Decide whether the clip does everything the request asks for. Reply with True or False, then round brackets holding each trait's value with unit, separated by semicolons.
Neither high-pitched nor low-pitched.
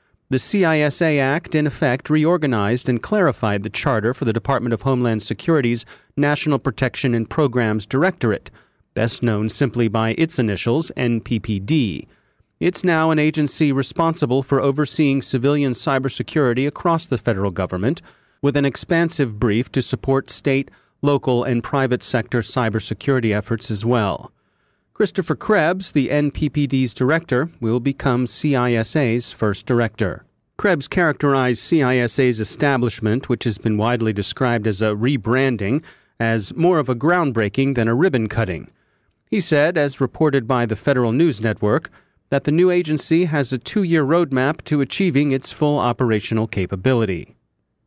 False (130 Hz)